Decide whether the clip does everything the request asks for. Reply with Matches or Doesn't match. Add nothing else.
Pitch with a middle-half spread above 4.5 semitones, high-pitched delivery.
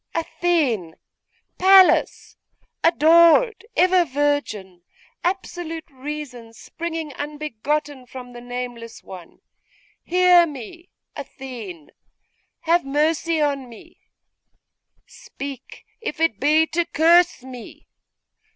Matches